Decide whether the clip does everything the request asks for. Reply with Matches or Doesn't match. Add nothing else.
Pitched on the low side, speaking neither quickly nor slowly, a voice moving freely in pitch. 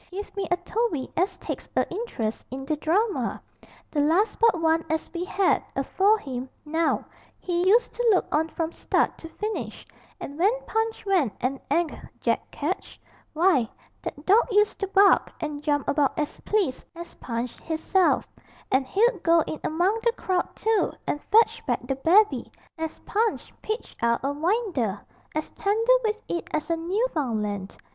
Doesn't match